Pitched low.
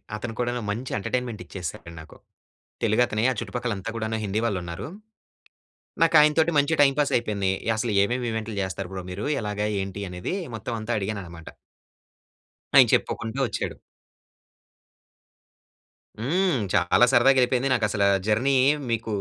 Yes: low, 110 Hz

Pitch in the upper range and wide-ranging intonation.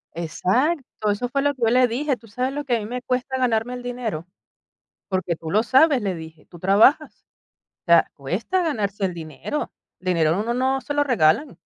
Yes: high, 235 Hz; wide, 6.1 semitones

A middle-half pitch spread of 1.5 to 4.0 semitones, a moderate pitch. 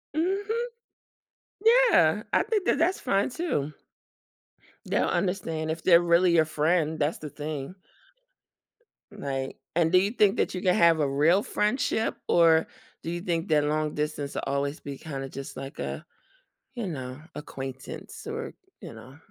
No: average, 4.9 semitones; medium, 160 Hz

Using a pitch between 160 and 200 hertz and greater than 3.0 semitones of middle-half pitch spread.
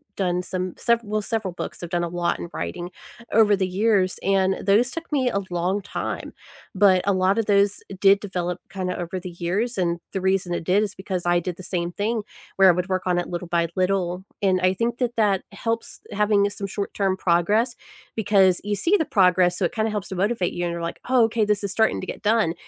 No: high, 190 Hz; average, 2.7 semitones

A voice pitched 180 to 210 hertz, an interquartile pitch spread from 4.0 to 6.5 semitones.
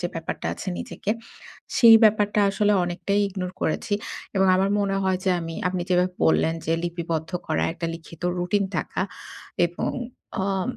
No: medium, 185 Hz; average, 2.7 semitones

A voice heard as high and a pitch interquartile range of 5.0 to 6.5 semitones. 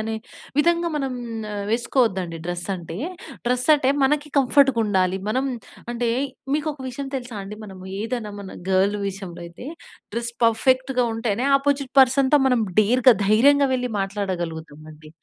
Yes: high, 235 Hz; wide, 5.4 semitones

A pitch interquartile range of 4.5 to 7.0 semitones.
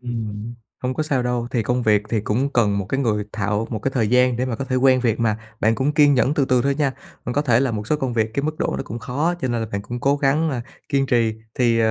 No: average, 3.4 semitones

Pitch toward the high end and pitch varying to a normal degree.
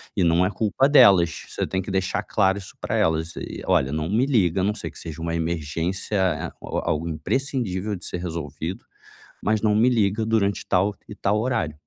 No: very low, 95 Hz; average, 4.2 semitones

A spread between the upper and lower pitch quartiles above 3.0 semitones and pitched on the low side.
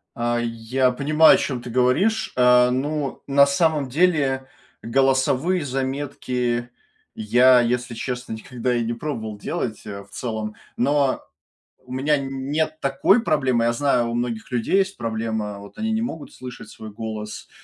Yes: average, 3.4 semitones; low, 125 Hz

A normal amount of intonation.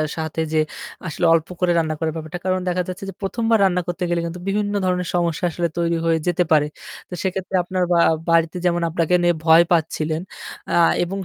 No: narrow, 1.9 semitones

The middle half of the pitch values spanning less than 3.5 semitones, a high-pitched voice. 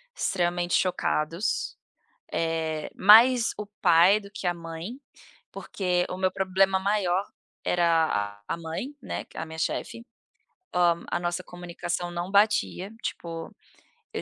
No: narrow, 2.6 semitones; medium, 175 Hz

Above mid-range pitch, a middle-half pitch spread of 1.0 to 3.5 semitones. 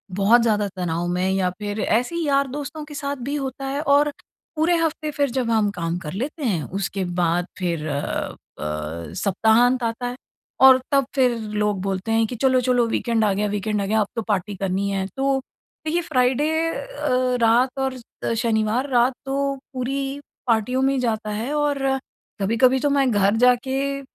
No: high, 240 Hz; average, 5.1 semitones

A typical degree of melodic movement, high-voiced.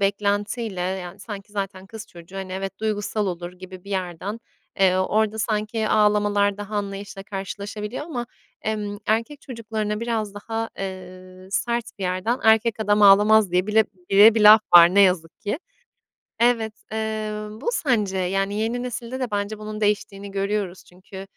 No: narrow, 2.2 semitones; high, 205 Hz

